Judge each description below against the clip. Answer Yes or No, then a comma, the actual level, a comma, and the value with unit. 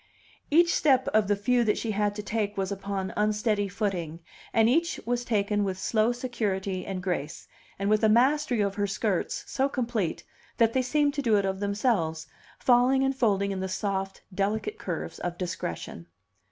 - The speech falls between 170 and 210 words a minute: Yes, average, 180 wpm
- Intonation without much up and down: No, average, 3.8 semitones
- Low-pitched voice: No, high, 210 Hz